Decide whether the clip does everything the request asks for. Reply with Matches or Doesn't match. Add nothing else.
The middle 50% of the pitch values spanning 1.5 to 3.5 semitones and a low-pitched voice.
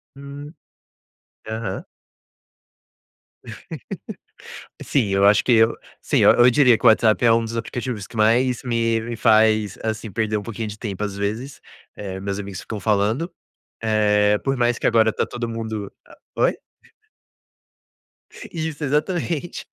Matches